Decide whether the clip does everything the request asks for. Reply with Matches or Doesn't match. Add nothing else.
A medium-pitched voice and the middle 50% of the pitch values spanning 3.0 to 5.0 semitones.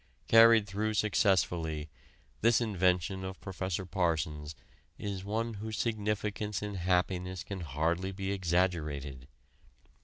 Doesn't match